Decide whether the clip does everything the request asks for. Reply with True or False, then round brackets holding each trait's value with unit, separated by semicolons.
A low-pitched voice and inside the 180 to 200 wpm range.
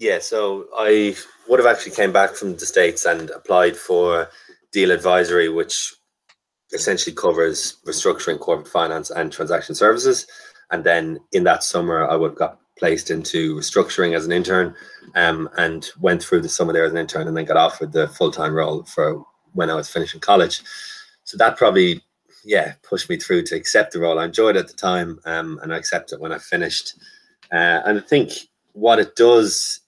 False (365 Hz; 190 wpm)